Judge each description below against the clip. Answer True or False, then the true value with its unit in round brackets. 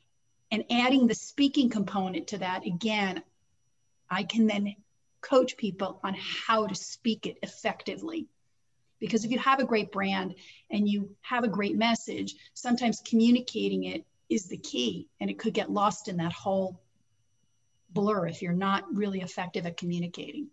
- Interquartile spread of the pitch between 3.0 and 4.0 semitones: False (4.4 semitones)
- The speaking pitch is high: True (200 Hz)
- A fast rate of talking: False (160 wpm)